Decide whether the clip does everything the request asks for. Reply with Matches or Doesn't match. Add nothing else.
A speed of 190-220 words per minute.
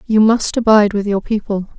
Matches